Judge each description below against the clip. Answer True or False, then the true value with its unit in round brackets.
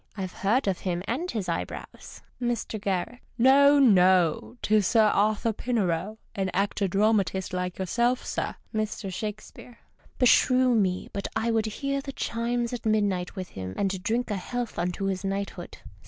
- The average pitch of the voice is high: True (210 Hz)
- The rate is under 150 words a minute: False (165 wpm)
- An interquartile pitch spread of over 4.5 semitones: False (3.9 semitones)